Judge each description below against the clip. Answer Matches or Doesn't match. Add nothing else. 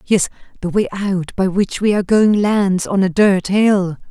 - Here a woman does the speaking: Matches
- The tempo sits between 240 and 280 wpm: Doesn't match